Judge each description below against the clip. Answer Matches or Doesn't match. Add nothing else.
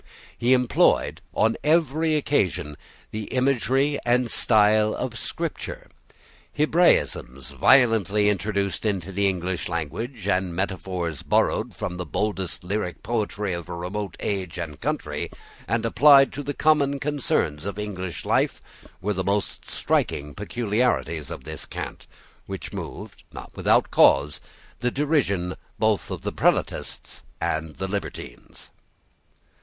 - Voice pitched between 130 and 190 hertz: Doesn't match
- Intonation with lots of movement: Matches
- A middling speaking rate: Doesn't match